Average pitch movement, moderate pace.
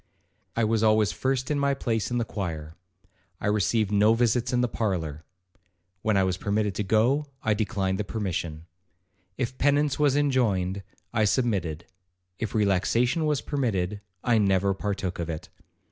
Yes: average, 4.5 semitones; average, 155 wpm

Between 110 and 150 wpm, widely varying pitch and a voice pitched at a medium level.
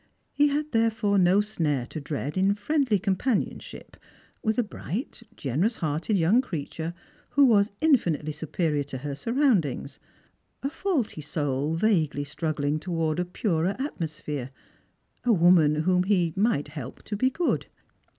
Yes: average, 140 wpm; wide, 6.5 semitones; medium, 180 Hz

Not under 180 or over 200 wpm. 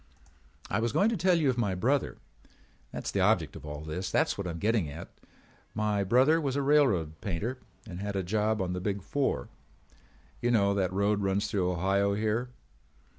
Yes: average, 190 wpm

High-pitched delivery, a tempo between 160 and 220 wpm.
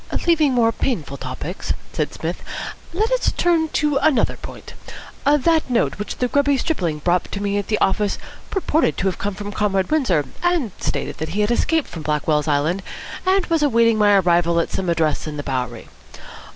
Yes: high, 205 Hz; average, 180 wpm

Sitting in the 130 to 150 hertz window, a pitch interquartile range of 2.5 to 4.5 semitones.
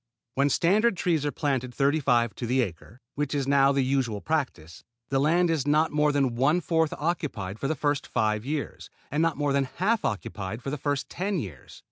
Yes: medium, 140 Hz; average, 3.8 semitones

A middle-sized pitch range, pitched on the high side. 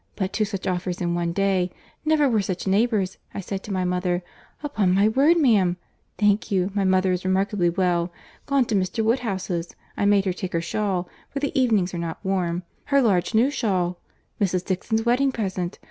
Yes: average, 3.5 semitones; high, 195 Hz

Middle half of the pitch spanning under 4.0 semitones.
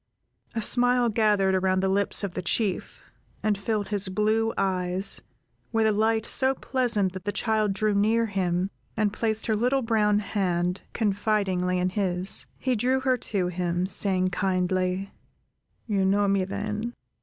Yes: average, 2.8 semitones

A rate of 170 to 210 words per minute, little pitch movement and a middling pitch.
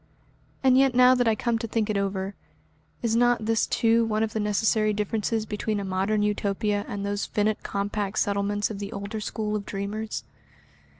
No: average, 185 wpm; narrow, 1.8 semitones; high, 210 Hz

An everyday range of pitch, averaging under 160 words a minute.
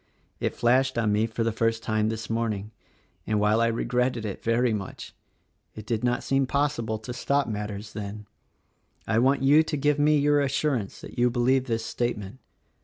No: average, 3.4 semitones; average, 180 wpm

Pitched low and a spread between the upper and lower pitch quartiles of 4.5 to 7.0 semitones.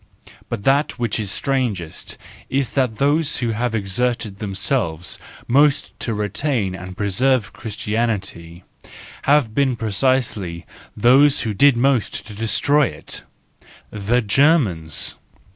Yes: low, 115 Hz; average, 5.0 semitones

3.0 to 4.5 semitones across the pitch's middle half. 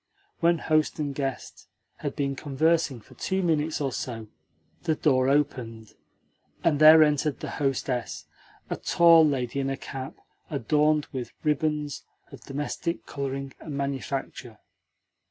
No: narrow, 2.5 semitones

